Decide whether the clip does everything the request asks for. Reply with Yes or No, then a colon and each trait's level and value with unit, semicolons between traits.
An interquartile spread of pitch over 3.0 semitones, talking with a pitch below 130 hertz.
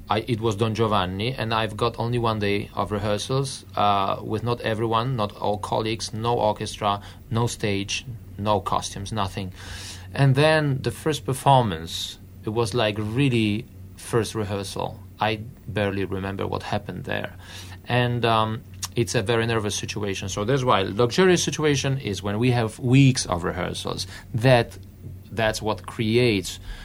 Yes: average, 3.5 semitones; low, 110 Hz